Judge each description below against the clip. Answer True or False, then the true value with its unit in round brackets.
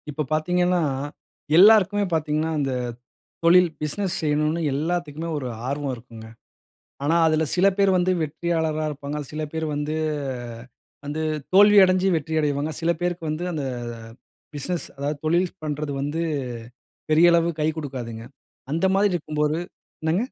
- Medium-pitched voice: True (155 Hz)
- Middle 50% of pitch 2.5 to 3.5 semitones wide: True (3.0 semitones)